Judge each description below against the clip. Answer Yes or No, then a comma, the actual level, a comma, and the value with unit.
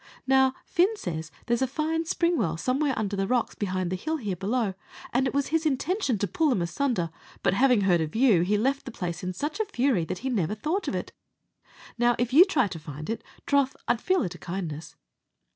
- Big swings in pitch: Yes, wide, 7.4 semitones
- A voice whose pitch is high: Yes, high, 240 Hz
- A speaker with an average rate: No, fast, 225 wpm